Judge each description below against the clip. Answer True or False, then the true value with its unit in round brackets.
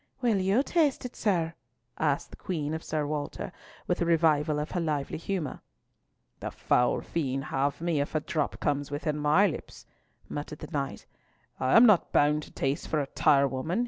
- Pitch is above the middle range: False (155 Hz)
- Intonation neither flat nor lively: True (3.2 semitones)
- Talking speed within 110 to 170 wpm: False (180 wpm)